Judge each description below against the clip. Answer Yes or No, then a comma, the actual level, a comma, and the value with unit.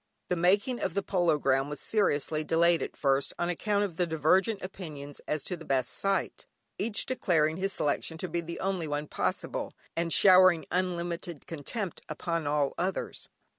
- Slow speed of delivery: No, average, 170 wpm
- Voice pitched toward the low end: No, medium, 170 Hz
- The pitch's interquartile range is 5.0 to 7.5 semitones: No, average, 3.6 semitones